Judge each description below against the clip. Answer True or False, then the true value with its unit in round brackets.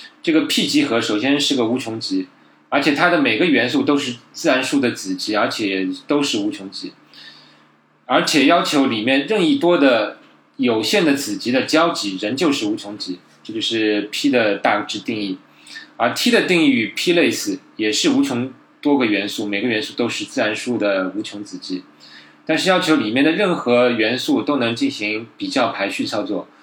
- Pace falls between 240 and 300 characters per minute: True (270 characters per minute)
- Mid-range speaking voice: True (145 Hz)